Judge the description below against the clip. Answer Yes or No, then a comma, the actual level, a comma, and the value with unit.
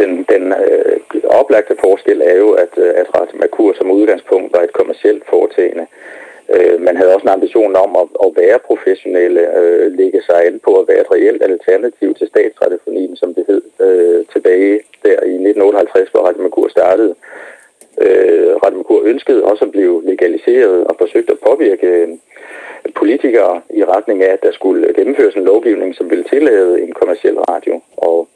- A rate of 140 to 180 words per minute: Yes, average, 175 wpm